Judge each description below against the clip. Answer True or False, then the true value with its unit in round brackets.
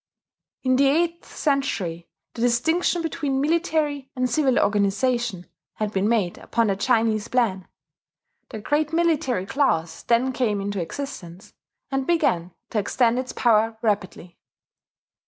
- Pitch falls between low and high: False (240 Hz)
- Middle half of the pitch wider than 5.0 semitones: True (5.5 semitones)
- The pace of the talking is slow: True (130 wpm)